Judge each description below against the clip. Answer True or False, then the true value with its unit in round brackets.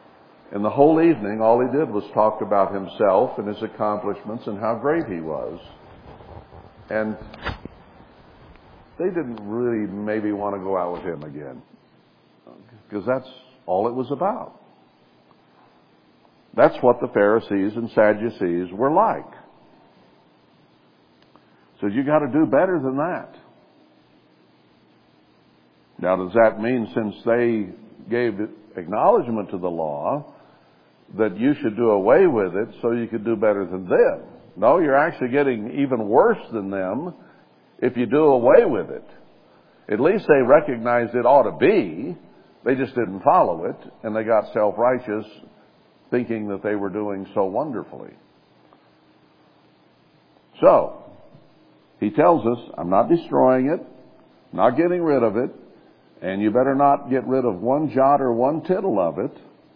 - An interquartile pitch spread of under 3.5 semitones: False (4.2 semitones)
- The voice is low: True (110 Hz)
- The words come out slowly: False (145 wpm)